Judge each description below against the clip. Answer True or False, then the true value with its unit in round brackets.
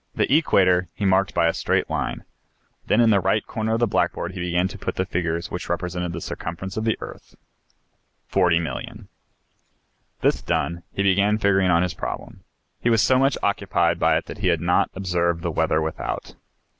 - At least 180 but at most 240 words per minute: True (190 wpm)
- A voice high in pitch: False (90 Hz)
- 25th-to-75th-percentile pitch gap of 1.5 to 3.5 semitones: True (2.7 semitones)